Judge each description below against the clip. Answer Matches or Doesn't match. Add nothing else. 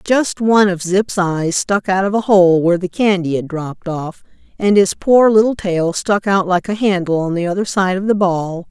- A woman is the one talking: Matches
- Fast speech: Matches